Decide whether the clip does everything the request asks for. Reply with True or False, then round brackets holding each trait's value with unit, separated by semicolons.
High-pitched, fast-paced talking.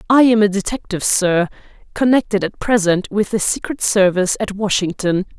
False (200 Hz; 155 wpm)